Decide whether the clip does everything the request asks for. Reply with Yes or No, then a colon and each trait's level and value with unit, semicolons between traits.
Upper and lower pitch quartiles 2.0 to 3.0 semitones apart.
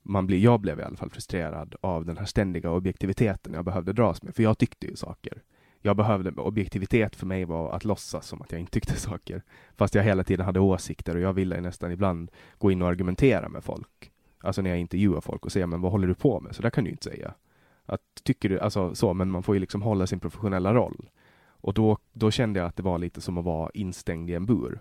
Yes: narrow, 2.6 semitones